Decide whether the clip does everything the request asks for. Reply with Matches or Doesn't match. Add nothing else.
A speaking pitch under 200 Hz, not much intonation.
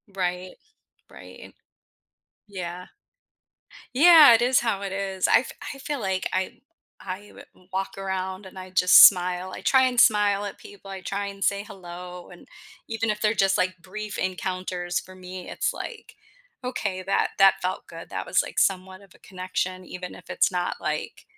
Matches